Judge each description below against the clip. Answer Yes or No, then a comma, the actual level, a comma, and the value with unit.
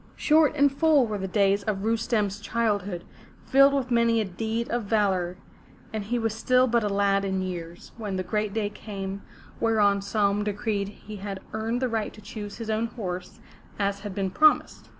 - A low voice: No, high, 210 Hz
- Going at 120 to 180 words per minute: No, average, 190 wpm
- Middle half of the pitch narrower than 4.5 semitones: Yes, narrow, 2.5 semitones